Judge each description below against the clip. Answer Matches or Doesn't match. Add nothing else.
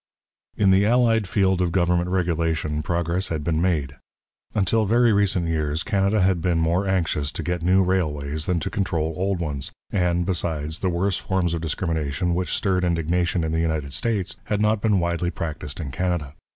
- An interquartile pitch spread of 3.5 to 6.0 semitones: Doesn't match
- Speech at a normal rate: Matches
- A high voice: Doesn't match